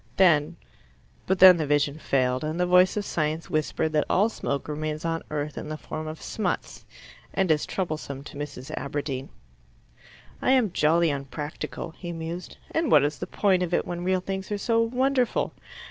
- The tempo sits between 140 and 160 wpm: No, average, 180 wpm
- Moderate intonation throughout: Yes, average, 3.8 semitones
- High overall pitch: No, medium, 165 Hz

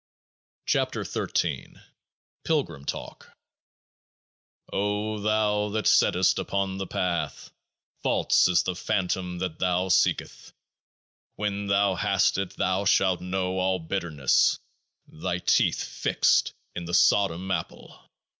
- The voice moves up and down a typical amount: No, narrow, 2.1 semitones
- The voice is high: No, very low, 95 Hz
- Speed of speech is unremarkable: No, slow, 115 wpm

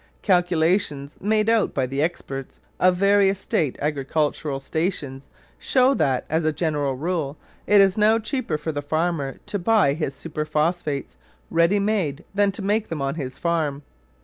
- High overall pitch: No, medium, 160 Hz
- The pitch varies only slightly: No, wide, 5.4 semitones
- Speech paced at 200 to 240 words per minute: No, average, 155 wpm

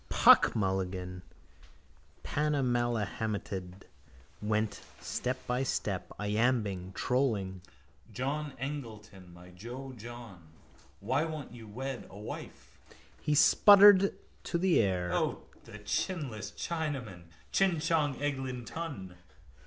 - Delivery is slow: Yes, slow, 105 wpm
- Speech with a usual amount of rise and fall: No, wide, 6.5 semitones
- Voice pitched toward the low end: Yes, low, 120 Hz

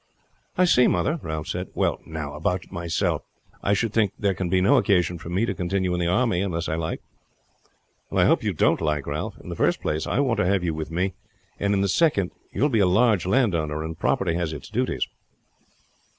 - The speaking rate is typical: No, fast, 220 wpm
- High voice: No, very low, 90 Hz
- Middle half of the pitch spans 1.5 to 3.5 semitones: No, average, 3.9 semitones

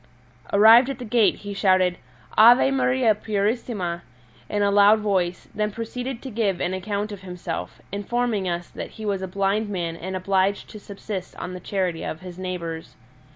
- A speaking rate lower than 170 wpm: No, average, 175 wpm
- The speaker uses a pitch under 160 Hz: No, high, 200 Hz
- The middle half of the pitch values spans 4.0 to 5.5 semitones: No, average, 2.9 semitones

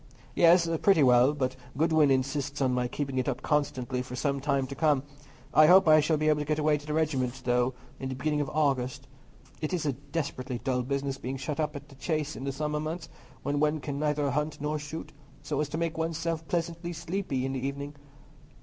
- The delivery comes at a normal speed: No, fast, 220 wpm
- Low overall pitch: No, medium, 145 Hz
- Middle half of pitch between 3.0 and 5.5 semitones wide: No, narrow, 2.5 semitones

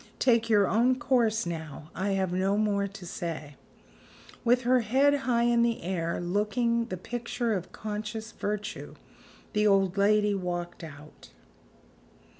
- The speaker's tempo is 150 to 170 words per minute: No, average, 140 wpm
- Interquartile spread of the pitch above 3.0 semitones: Yes, average, 4.2 semitones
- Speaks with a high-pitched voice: Yes, high, 210 Hz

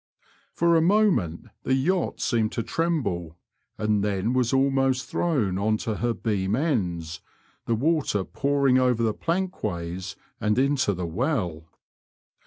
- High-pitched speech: No, low, 115 Hz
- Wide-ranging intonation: Yes, wide, 6.4 semitones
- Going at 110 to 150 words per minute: Yes, slow, 135 wpm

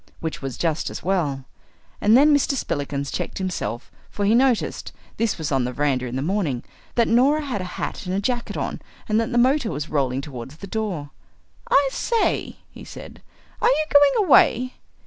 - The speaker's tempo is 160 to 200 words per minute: Yes, average, 185 wpm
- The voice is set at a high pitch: Yes, high, 195 Hz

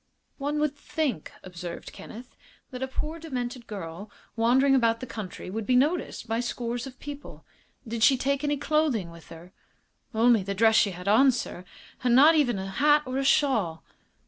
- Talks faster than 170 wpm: Yes, average, 180 wpm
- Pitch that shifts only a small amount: No, average, 5.1 semitones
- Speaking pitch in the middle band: No, high, 245 Hz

